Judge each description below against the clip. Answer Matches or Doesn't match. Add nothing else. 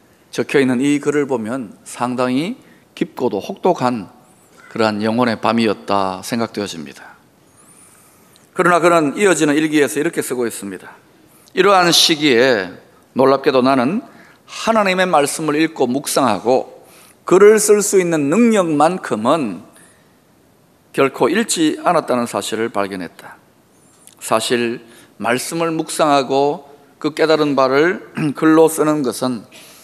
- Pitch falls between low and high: Matches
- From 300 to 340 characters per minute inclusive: Doesn't match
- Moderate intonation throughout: Doesn't match